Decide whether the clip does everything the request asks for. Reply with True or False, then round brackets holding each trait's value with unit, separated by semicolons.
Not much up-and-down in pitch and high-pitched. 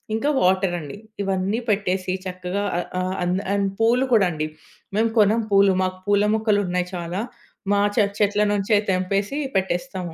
True (2.1 semitones; 195 Hz)